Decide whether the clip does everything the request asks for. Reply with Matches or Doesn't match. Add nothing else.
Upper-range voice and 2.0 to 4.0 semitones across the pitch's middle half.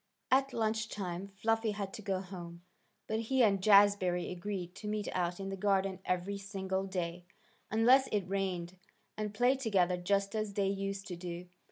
Matches